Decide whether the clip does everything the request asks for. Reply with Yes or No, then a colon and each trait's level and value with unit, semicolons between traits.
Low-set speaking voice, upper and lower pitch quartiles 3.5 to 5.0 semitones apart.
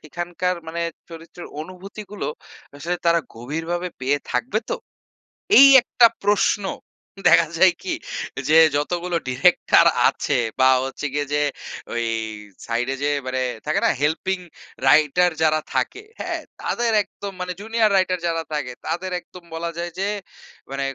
No: medium, 170 Hz; average, 4.0 semitones